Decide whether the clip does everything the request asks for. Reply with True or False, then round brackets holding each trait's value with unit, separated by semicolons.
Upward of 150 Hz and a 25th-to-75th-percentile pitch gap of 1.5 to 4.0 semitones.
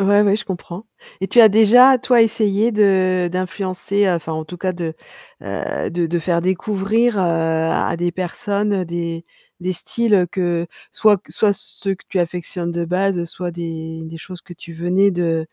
True (185 Hz; 3.0 semitones)